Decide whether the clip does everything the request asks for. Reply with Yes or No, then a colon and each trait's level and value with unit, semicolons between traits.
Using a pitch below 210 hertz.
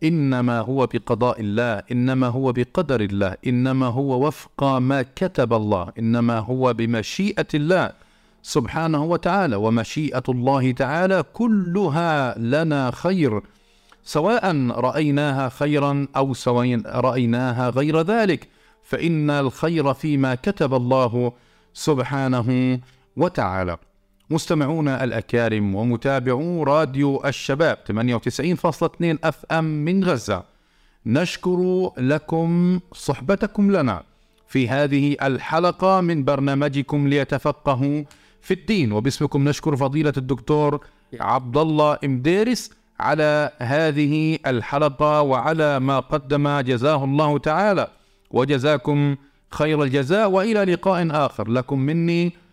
Yes: medium, 140 Hz